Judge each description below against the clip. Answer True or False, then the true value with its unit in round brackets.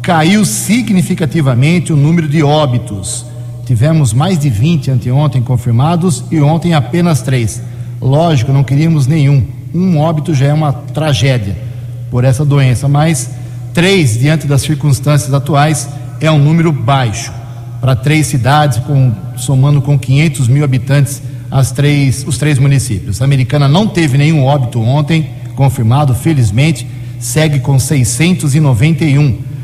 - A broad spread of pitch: False (3.5 semitones)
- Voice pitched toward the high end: False (140 Hz)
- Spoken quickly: False (130 wpm)